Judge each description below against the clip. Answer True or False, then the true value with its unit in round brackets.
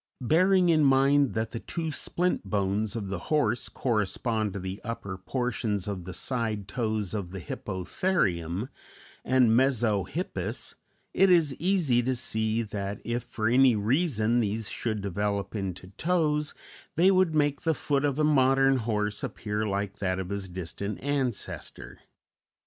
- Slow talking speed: False (150 wpm)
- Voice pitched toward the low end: True (115 Hz)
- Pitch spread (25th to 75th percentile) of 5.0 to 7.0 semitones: True (5.6 semitones)